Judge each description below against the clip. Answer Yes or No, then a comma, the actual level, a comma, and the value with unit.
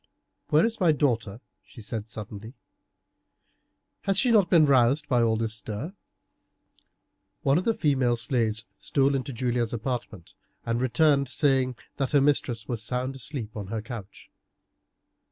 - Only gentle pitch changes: No, average, 4.0 semitones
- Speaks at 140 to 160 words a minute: Yes, average, 145 wpm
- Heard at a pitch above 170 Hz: No, low, 125 Hz